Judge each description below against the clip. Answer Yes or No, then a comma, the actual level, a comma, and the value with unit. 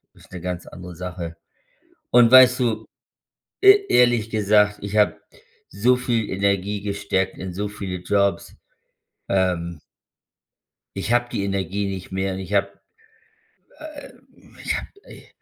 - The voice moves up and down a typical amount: Yes, average, 3.3 semitones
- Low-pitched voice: Yes, low, 100 Hz